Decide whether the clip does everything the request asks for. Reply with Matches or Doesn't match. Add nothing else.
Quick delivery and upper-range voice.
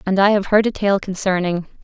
Matches